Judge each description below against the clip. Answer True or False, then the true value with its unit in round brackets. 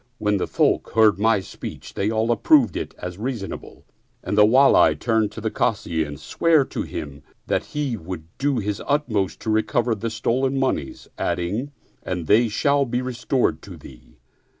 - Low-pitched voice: True (110 Hz)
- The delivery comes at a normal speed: True (175 wpm)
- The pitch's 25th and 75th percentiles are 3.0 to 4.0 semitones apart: False (4.4 semitones)